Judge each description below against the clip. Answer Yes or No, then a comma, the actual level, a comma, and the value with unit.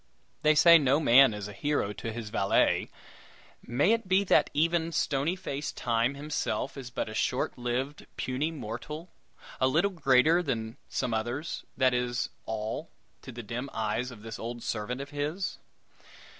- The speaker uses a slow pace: No, average, 165 wpm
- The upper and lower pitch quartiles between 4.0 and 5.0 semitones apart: Yes, average, 4.6 semitones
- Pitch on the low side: Yes, low, 130 Hz